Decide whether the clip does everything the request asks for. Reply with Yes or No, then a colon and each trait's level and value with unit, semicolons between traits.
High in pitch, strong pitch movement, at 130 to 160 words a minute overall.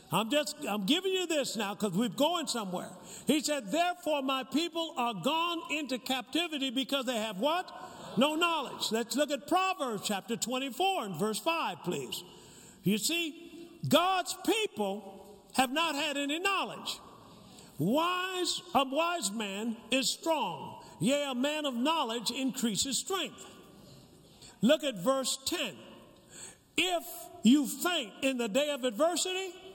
Yes: very high, 280 Hz; wide, 6.1 semitones; slow, 135 wpm